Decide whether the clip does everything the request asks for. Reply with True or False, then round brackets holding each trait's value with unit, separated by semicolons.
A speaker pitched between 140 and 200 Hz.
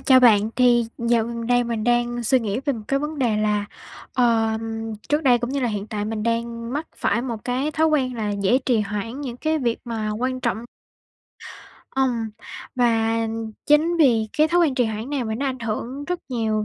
False (240 Hz)